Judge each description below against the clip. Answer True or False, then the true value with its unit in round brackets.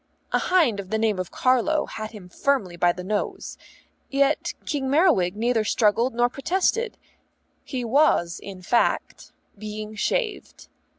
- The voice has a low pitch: False (230 Hz)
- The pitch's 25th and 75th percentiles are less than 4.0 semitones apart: False (5.3 semitones)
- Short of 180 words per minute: True (140 wpm)